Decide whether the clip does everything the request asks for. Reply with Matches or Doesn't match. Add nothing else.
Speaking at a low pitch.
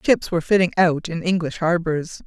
Doesn't match